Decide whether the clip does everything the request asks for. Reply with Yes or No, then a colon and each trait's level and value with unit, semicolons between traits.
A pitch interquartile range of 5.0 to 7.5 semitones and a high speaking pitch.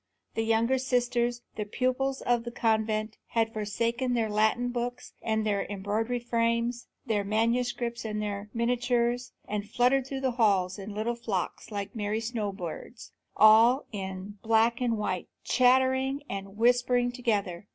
No: narrow, 2.6 semitones; high, 230 Hz